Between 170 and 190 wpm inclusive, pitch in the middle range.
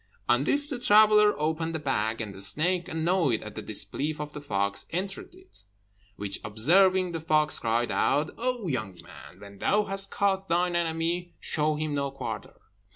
Yes: average, 175 wpm; medium, 160 Hz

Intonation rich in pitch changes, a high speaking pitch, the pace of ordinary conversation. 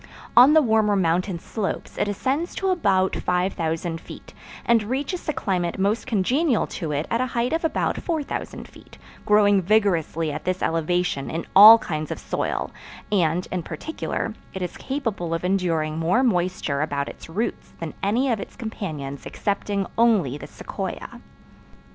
Yes: wide, 5.8 semitones; high, 195 Hz; average, 160 wpm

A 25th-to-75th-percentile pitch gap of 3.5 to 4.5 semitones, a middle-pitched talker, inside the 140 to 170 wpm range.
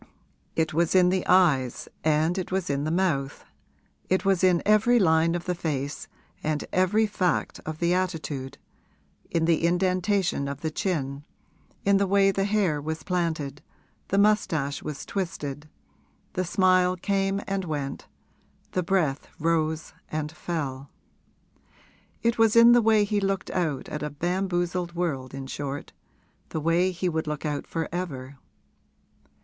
Yes: average, 3.8 semitones; medium, 170 Hz; average, 150 wpm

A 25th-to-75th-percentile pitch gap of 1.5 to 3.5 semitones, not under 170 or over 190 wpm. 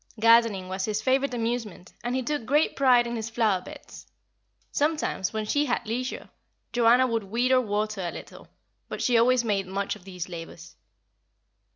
No: average, 4.1 semitones; average, 175 wpm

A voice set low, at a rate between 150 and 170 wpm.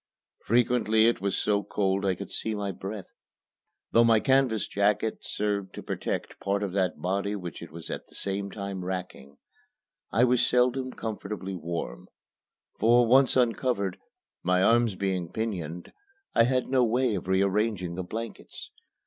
Yes: low, 100 Hz; average, 155 wpm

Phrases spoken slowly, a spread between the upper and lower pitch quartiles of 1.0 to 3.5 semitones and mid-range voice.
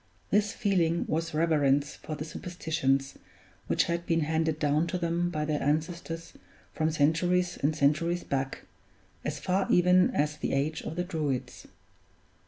No: average, 150 wpm; average, 2.7 semitones; medium, 160 Hz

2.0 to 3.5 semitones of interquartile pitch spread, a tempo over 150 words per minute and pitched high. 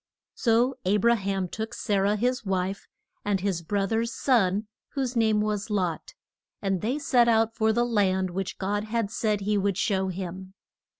Yes: average, 2.9 semitones; average, 180 wpm; high, 205 Hz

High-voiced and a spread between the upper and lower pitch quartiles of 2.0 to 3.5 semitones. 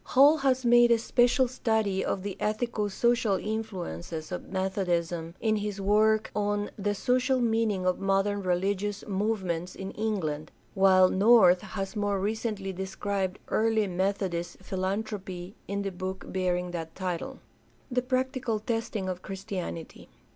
Yes: high, 200 Hz; average, 2.9 semitones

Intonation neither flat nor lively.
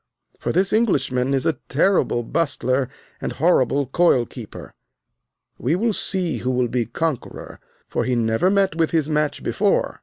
No: wide, 5.7 semitones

